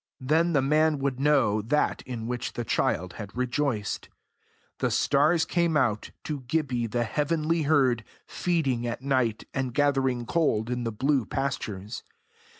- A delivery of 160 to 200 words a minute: No, average, 150 wpm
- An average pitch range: Yes, average, 3.9 semitones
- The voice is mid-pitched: No, low, 130 Hz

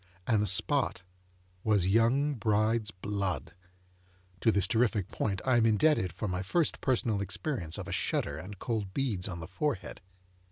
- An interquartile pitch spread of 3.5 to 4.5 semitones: Yes, average, 4.0 semitones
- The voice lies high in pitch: No, low, 105 Hz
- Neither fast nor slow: Yes, average, 160 wpm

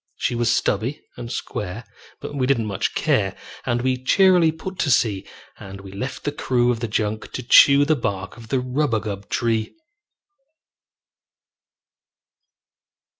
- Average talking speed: Yes, average, 145 wpm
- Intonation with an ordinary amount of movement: Yes, average, 4.1 semitones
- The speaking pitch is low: Yes, low, 120 Hz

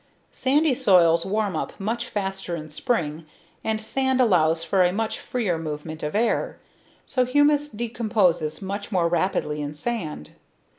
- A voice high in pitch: Yes, high, 195 Hz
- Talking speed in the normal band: Yes, average, 145 wpm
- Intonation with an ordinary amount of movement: No, wide, 6.3 semitones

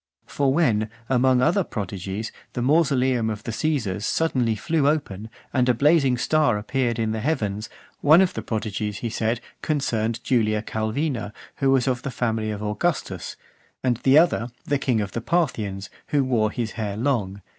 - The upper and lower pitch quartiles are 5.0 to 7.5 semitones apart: No, average, 4.3 semitones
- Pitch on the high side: No, low, 120 Hz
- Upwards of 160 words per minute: Yes, average, 170 wpm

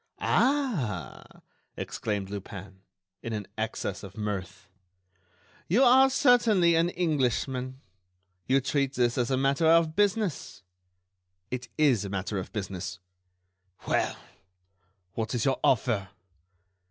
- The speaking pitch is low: Yes, low, 125 Hz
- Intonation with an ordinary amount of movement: No, wide, 8.3 semitones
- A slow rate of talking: Yes, slow, 115 wpm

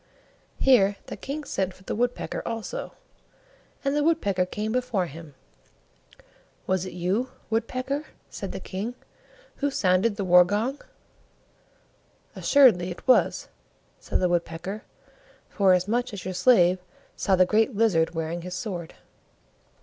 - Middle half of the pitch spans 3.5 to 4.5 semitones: No, average, 5.2 semitones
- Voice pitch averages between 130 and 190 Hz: No, high, 200 Hz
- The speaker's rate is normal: No, slow, 130 wpm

